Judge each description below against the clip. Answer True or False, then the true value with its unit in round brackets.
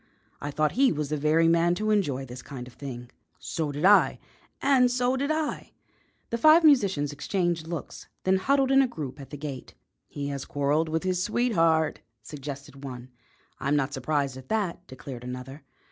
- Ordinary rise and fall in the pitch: False (6.6 semitones)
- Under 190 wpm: True (180 wpm)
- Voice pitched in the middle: True (155 Hz)